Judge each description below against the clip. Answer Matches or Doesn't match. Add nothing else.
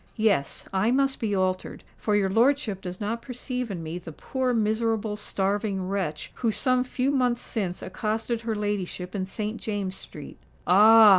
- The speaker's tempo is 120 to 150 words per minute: Doesn't match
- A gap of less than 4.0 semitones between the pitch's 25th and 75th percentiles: Matches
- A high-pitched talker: Matches